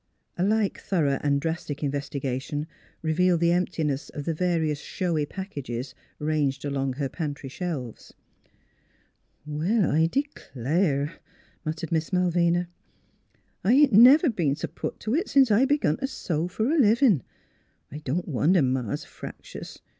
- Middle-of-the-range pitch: Yes, medium, 160 Hz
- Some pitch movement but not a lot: Yes, average, 5.0 semitones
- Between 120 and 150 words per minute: Yes, average, 140 wpm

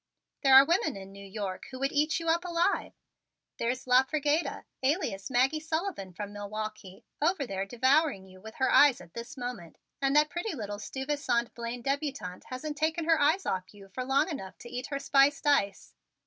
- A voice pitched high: Yes, very high, 265 Hz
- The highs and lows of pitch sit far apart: Yes, wide, 6.5 semitones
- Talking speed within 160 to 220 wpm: Yes, average, 190 wpm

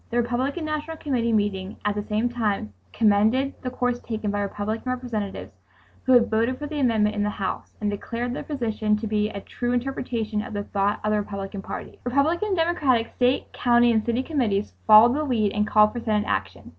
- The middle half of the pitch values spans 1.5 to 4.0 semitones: Yes, average, 3.3 semitones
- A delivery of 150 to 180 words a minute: No, fast, 205 wpm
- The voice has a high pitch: Yes, high, 230 Hz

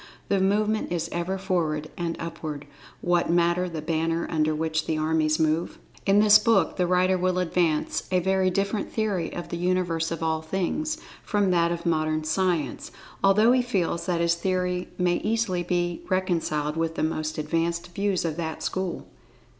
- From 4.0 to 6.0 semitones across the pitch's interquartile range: No, narrow, 2.6 semitones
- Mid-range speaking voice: Yes, medium, 175 Hz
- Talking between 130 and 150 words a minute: No, average, 170 wpm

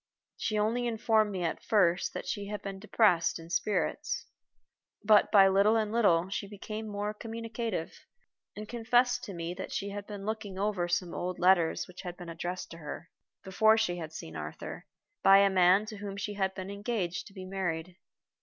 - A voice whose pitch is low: No, high, 195 Hz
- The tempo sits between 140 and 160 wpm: No, average, 190 wpm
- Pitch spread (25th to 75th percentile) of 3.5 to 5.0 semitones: No, average, 3.1 semitones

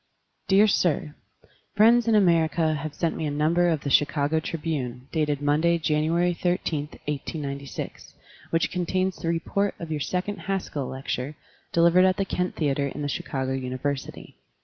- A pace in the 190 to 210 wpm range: No, average, 150 wpm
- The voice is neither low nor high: Yes, medium, 160 Hz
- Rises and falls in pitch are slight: No, average, 3.6 semitones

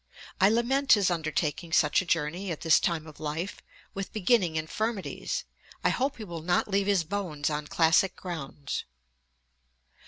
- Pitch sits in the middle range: Yes, medium, 175 Hz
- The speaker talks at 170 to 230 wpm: No, average, 155 wpm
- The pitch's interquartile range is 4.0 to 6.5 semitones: Yes, average, 4.3 semitones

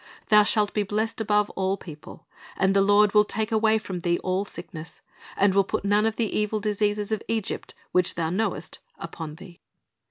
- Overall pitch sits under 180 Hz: No, high, 205 Hz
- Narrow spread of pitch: Yes, narrow, 2.1 semitones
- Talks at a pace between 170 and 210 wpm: Yes, average, 190 wpm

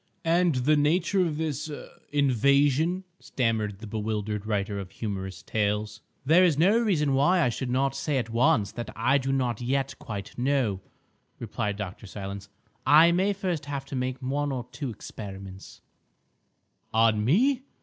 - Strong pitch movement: Yes, wide, 5.9 semitones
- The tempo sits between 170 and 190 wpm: No, average, 150 wpm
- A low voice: Yes, low, 130 Hz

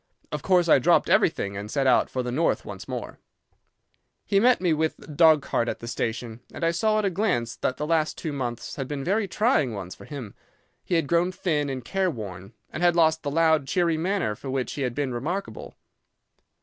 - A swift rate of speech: Yes, fast, 215 wpm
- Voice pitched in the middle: Yes, medium, 150 Hz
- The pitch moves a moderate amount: No, wide, 5.8 semitones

